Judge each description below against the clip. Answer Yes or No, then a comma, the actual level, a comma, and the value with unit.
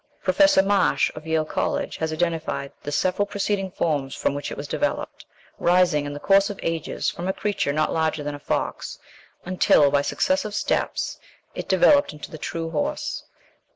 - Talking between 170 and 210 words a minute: Yes, average, 175 wpm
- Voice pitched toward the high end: No, medium, 165 Hz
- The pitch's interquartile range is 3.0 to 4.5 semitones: No, average, 4.9 semitones